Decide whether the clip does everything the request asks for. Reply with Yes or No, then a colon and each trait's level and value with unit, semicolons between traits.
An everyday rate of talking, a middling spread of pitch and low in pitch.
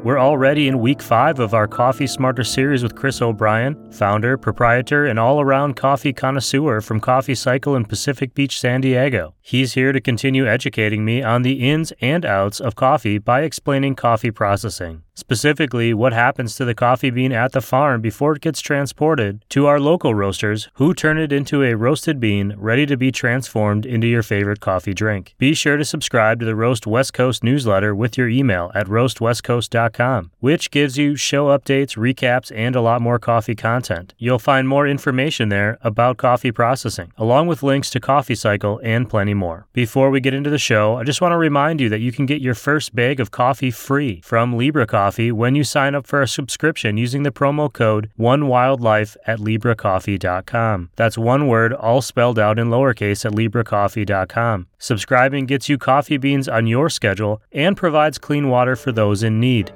Yes: average, 190 wpm; average, 3.8 semitones; low, 125 Hz